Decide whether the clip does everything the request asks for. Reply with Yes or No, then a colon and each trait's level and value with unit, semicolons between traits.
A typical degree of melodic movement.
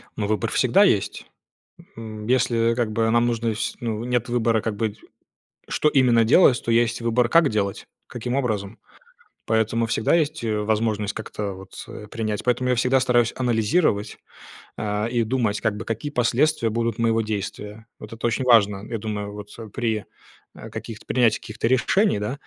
No: narrow, 2.2 semitones